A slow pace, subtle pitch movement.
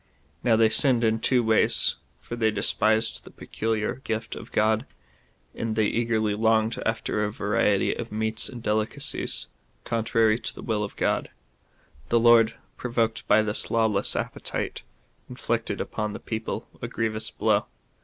No: average, 155 wpm; narrow, 1.1 semitones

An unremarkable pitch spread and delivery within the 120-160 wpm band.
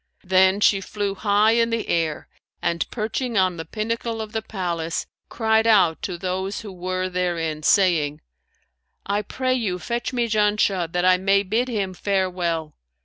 Yes: average, 3.6 semitones; average, 155 wpm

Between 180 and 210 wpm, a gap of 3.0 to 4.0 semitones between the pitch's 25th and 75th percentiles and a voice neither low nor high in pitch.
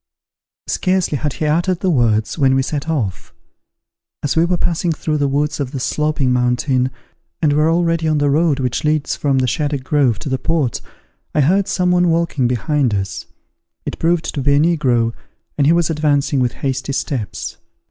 Yes: average, 190 wpm; average, 3.7 semitones; medium, 145 Hz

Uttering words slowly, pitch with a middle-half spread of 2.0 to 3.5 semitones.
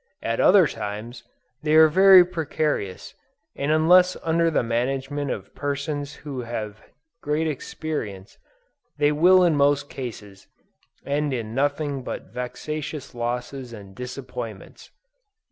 No: slow, 120 wpm; average, 4.5 semitones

